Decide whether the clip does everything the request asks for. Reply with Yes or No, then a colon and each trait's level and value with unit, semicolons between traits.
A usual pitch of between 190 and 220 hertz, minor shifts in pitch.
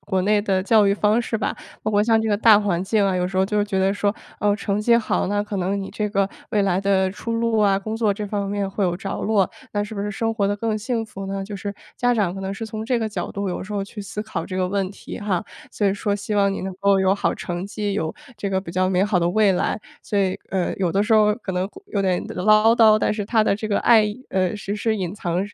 Yes: high, 205 Hz; narrow, 1.8 semitones